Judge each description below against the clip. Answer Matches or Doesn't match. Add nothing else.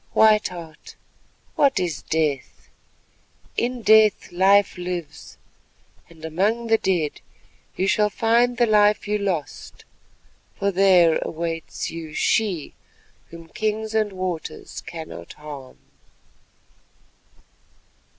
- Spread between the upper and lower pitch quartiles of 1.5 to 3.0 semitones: Doesn't match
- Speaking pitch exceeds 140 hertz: Matches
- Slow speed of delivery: Matches